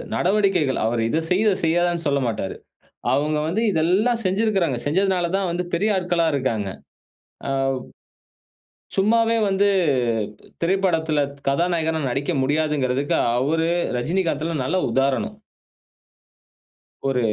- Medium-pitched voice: Yes, medium, 165 Hz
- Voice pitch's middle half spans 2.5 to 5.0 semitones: No, wide, 5.4 semitones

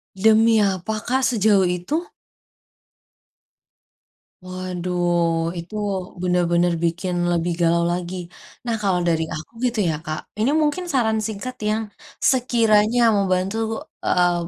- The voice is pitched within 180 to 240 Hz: Yes, high, 190 Hz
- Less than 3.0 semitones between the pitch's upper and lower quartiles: No, average, 4.0 semitones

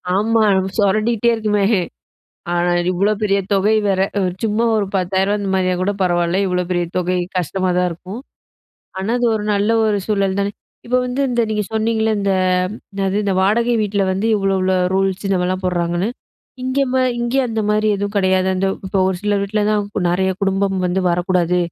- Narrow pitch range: Yes, narrow, 2.3 semitones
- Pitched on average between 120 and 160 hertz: No, high, 195 Hz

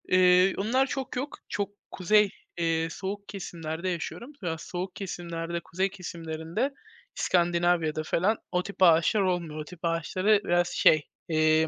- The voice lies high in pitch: No, medium, 175 Hz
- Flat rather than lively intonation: No, average, 3.0 semitones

